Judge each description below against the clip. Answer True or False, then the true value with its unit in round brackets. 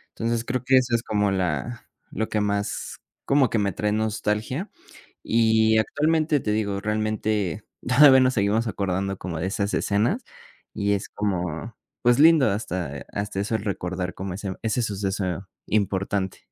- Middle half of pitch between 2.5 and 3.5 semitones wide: True (2.9 semitones)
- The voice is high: False (105 Hz)